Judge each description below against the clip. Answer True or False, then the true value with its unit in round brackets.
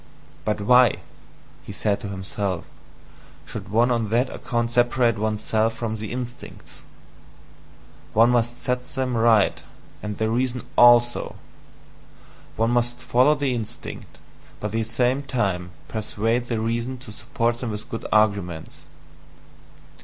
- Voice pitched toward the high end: False (115 Hz)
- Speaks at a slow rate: True (130 wpm)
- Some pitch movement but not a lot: False (2.3 semitones)